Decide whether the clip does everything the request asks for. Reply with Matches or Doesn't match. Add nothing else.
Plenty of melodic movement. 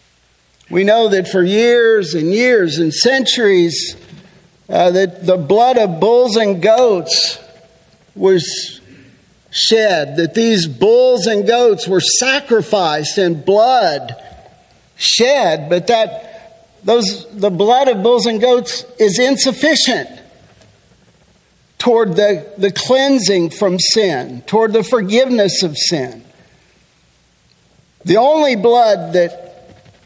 Doesn't match